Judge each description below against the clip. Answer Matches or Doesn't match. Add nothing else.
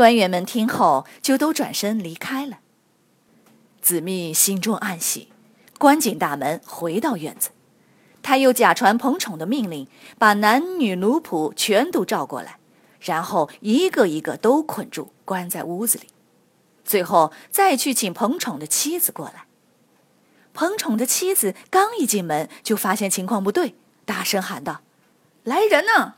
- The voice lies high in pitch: Matches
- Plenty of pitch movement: Matches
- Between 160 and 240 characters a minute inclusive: Matches